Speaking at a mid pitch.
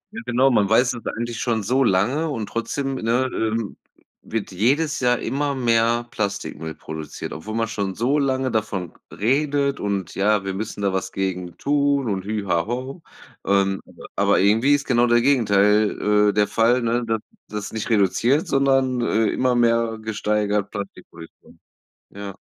No: low, 115 Hz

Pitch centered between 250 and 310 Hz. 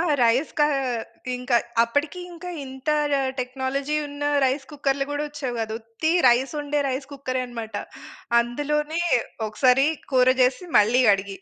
Yes: very high, 265 Hz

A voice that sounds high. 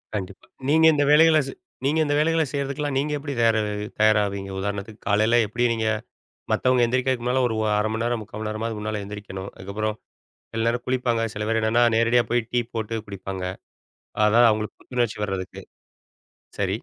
No: low, 115 Hz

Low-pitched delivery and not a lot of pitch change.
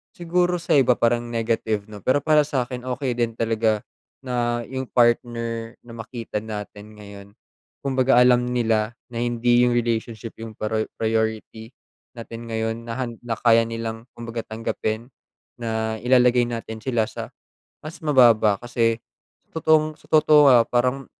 Yes: low, 115 Hz; narrow, 1.9 semitones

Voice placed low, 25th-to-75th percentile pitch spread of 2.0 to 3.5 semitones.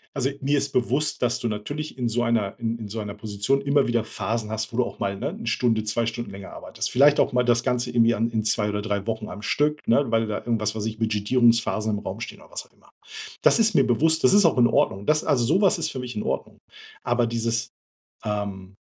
Yes: low, 115 Hz; average, 2.8 semitones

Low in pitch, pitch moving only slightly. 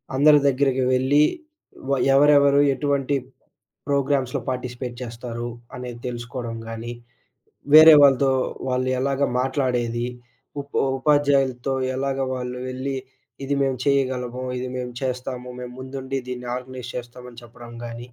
Yes: low, 130 Hz; narrow, 1.9 semitones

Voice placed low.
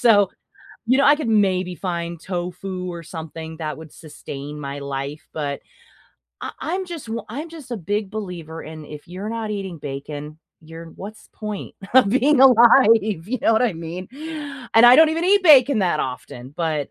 No: medium, 185 Hz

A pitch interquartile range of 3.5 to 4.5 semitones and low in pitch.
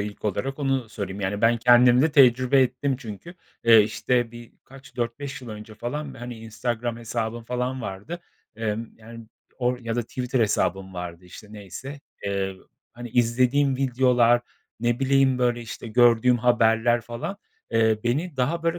No: narrow, 2.4 semitones; low, 120 Hz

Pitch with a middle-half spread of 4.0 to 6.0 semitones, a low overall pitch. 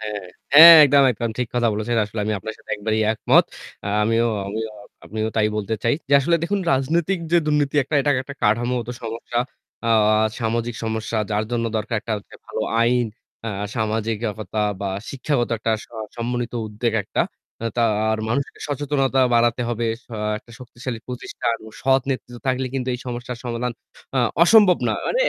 No: average, 3.0 semitones; low, 120 Hz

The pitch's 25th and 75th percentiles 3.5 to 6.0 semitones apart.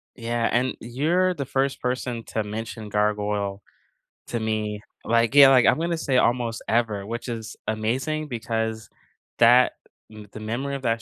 No: average, 3.0 semitones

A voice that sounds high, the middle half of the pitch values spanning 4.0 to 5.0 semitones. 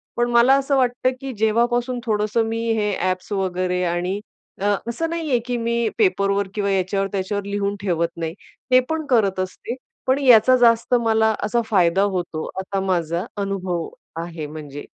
Yes: high, 205 Hz; average, 4.4 semitones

